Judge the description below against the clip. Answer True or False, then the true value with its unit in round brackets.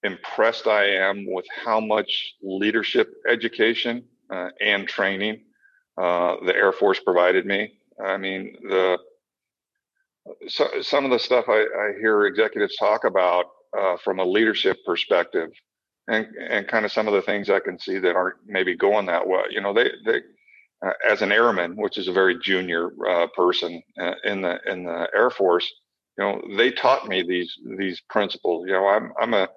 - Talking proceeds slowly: False (180 wpm)